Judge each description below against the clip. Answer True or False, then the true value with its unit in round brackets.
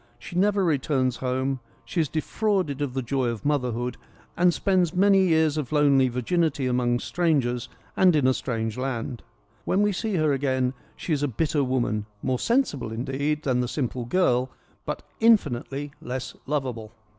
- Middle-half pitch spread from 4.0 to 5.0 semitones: True (4.3 semitones)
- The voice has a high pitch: False (135 Hz)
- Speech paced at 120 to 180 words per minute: True (170 wpm)